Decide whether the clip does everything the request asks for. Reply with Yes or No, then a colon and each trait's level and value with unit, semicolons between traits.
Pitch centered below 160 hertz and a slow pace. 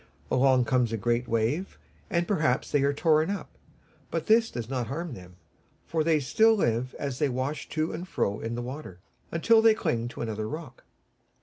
No: low, 135 Hz; average, 190 wpm